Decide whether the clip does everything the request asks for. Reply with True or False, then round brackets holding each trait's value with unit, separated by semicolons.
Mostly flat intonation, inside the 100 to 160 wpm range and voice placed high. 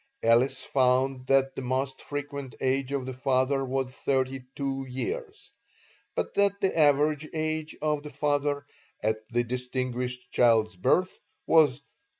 False (2.3 semitones; 145 wpm; 135 Hz)